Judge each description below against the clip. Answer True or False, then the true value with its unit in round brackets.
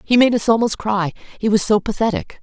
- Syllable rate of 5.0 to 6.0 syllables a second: True (5.5 syllables/s)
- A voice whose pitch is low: False (215 Hz)